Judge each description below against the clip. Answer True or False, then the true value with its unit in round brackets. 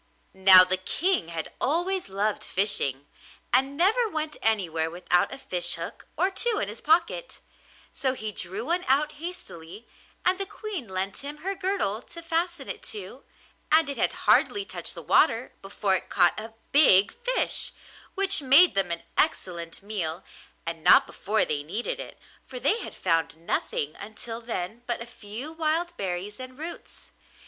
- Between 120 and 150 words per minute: False (165 wpm)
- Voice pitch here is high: True (235 Hz)